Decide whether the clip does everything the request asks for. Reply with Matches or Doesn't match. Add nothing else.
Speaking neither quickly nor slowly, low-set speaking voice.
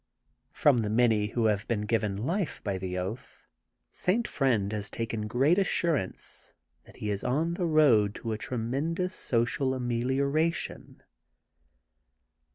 Doesn't match